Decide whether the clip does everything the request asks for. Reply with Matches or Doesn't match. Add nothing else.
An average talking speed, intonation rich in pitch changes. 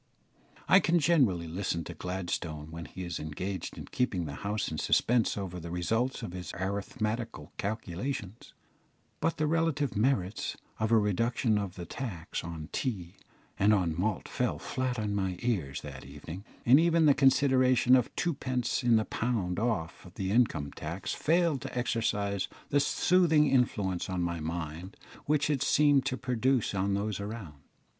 Matches